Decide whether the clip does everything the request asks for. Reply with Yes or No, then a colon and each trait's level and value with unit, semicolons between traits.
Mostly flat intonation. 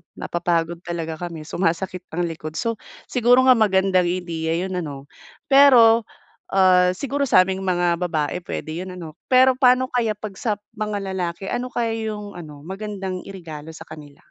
No: average, 4.5 semitones